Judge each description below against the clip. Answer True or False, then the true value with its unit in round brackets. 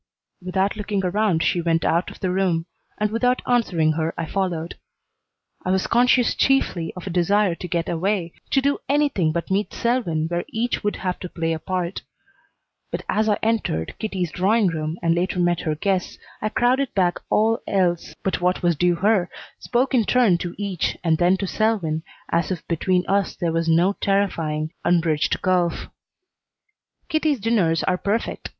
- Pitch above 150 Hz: True (185 Hz)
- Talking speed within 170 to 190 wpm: True (175 wpm)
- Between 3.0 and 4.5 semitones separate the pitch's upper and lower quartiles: True (3.9 semitones)